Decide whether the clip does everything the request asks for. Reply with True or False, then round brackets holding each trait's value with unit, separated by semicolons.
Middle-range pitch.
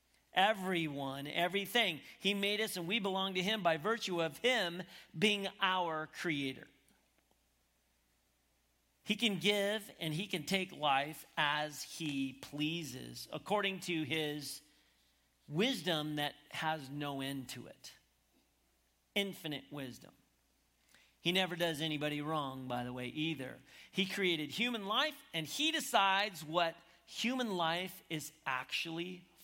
True (160 Hz)